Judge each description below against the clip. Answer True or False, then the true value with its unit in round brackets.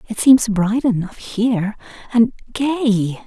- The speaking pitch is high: True (220 Hz)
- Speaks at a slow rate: True (130 wpm)